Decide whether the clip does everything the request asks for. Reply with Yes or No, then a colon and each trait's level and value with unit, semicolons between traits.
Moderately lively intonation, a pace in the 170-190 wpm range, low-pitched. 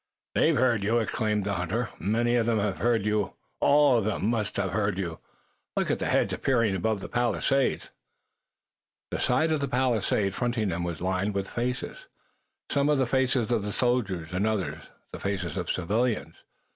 Yes: average, 3.9 semitones; average, 175 wpm; low, 110 Hz